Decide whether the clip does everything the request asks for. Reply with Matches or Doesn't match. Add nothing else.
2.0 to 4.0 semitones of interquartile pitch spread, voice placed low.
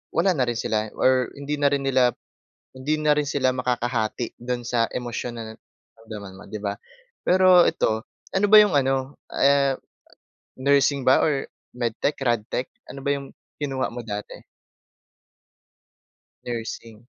Matches